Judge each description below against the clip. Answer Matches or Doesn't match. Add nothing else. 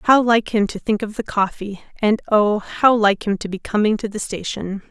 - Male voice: Doesn't match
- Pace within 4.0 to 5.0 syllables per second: Matches